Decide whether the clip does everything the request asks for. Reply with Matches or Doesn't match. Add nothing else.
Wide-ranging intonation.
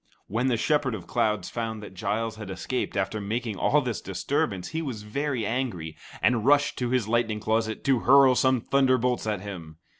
Doesn't match